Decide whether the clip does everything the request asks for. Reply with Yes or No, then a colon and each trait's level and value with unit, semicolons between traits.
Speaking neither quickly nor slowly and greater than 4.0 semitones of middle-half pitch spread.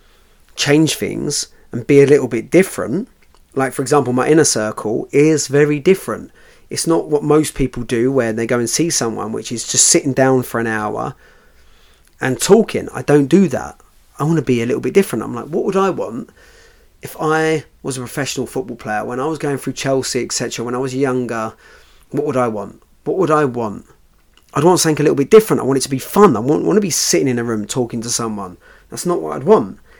No: fast, 230 wpm; average, 4.4 semitones